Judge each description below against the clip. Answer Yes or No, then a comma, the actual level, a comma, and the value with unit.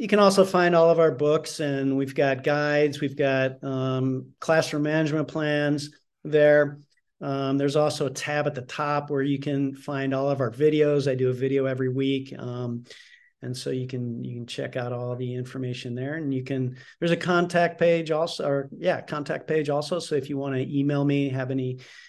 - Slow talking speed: No, fast, 205 wpm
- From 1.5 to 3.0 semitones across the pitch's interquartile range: Yes, narrow, 2.5 semitones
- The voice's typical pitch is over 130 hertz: Yes, medium, 140 Hz